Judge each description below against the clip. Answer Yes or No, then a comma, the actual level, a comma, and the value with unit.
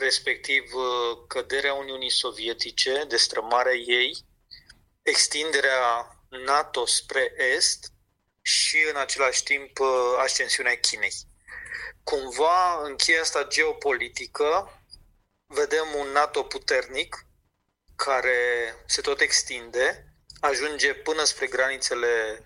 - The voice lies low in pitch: No, medium, 155 Hz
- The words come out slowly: Yes, slow, 90 wpm